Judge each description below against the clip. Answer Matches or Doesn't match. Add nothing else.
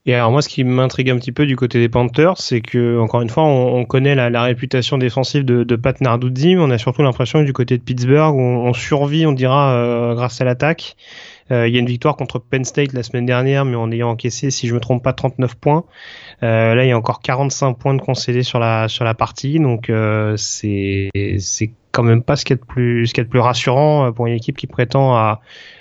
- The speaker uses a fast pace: Matches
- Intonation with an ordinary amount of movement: Doesn't match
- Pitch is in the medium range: Doesn't match